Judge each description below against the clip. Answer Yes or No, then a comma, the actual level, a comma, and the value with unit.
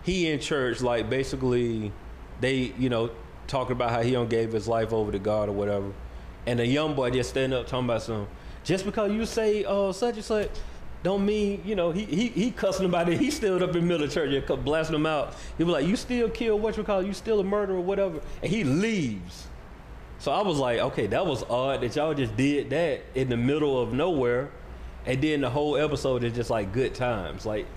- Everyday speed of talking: No, fast, 235 wpm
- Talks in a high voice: No, low, 135 Hz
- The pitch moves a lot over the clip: Yes, wide, 8.1 semitones